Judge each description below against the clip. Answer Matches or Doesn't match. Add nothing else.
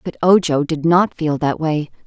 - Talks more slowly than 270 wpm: Matches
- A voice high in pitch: Doesn't match